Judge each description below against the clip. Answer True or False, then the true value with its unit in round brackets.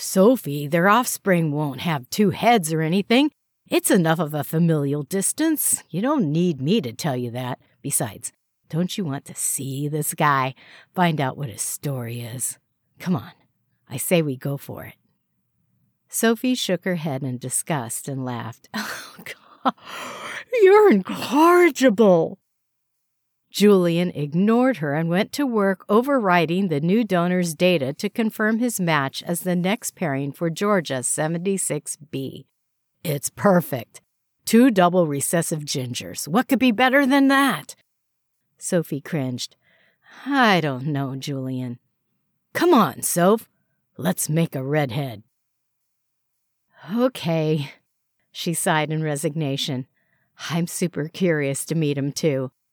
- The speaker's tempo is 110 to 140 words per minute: True (135 wpm)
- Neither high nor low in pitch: True (165 Hz)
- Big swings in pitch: True (6.2 semitones)